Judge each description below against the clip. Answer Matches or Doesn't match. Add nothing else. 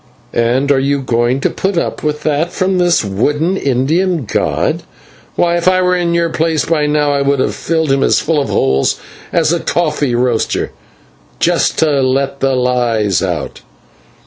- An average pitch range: Matches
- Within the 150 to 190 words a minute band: Matches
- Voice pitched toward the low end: Doesn't match